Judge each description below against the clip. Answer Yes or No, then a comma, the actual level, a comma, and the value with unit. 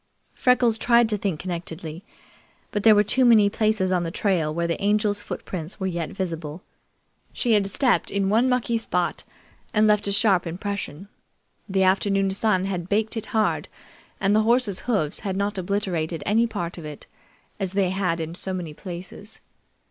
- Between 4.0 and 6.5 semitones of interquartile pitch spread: No, average, 3.3 semitones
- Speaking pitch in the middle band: No, high, 195 Hz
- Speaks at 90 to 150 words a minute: No, average, 175 wpm